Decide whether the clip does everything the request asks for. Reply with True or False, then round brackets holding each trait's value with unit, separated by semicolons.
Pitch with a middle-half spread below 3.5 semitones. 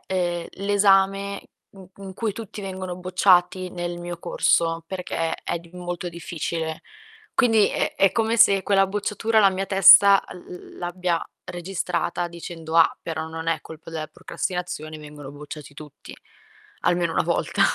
True (2.8 semitones)